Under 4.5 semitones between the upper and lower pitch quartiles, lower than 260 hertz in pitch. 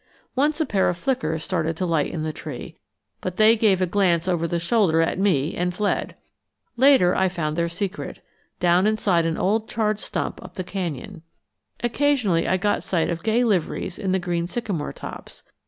Yes: average, 4.0 semitones; medium, 185 Hz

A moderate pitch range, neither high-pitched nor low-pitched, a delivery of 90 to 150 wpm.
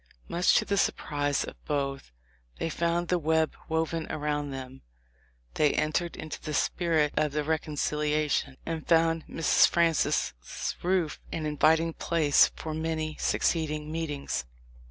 No: narrow, 1.7 semitones; medium, 155 Hz; slow, 135 wpm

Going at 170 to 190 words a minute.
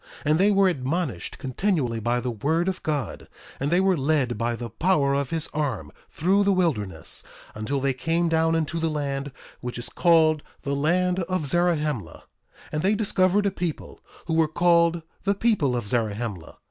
Yes: average, 180 wpm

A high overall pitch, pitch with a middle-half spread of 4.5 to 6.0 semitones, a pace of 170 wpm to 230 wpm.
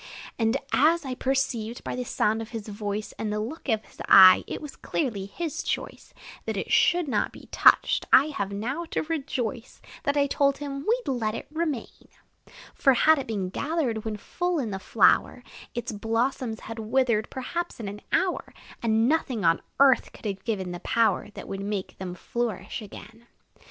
Yes: high, 235 Hz; average, 4.8 semitones; average, 185 wpm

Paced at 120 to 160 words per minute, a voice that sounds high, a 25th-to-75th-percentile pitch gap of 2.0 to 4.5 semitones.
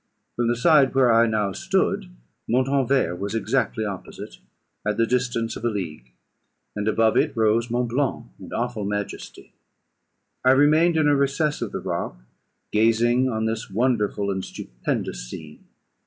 No: average, 155 wpm; low, 115 Hz; average, 3.8 semitones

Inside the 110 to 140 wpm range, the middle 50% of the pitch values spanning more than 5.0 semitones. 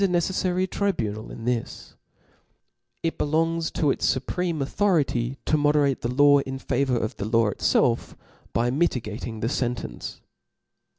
Yes: slow, 135 wpm; wide, 5.6 semitones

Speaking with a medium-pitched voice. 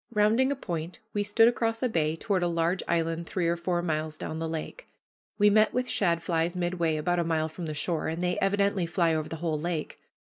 Yes: medium, 170 Hz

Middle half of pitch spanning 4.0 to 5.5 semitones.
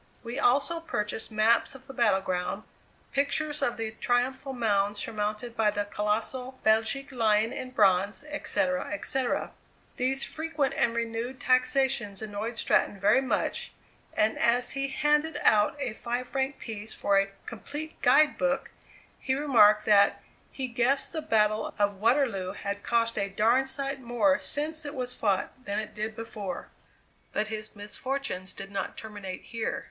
Yes: average, 4.3 semitones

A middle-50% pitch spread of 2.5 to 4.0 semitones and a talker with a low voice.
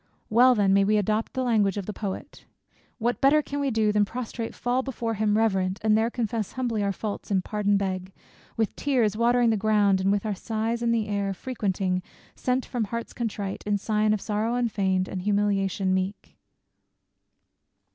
No: average, 2.8 semitones; high, 215 Hz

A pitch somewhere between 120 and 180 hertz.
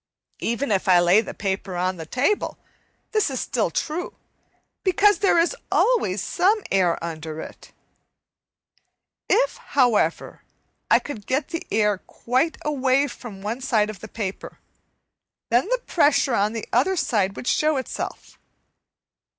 No: high, 245 Hz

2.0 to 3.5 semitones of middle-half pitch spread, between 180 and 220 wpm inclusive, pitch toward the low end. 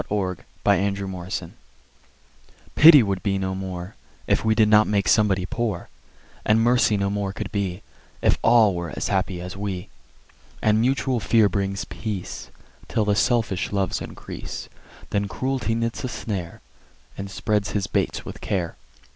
No: narrow, 2.6 semitones; average, 155 wpm; low, 100 Hz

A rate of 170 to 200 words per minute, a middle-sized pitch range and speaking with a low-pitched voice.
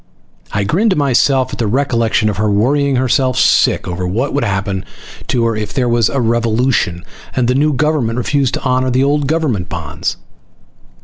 Yes: average, 190 wpm; average, 4.3 semitones; low, 125 Hz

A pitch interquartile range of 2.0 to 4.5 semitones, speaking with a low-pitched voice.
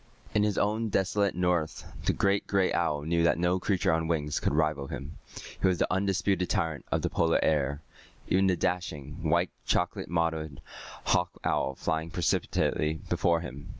Yes: average, 3.3 semitones; very low, 85 Hz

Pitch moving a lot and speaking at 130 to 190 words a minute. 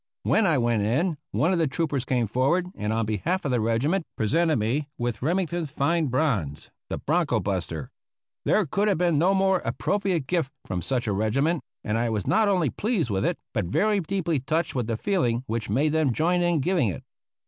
No: wide, 7.0 semitones; fast, 205 wpm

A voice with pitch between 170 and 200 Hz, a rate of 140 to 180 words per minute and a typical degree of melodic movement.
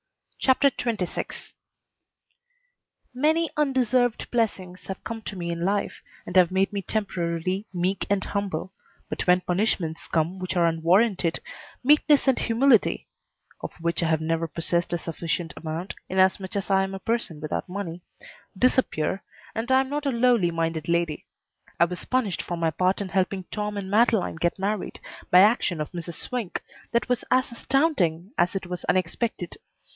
Yes: high, 190 Hz; average, 160 wpm; average, 5.0 semitones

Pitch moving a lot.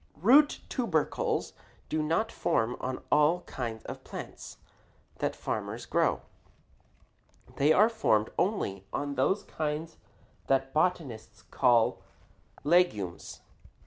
Yes: wide, 6.1 semitones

